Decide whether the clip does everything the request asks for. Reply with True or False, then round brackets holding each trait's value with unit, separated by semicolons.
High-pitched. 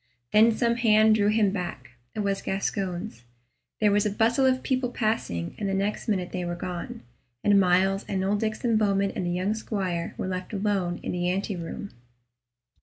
True (200 Hz)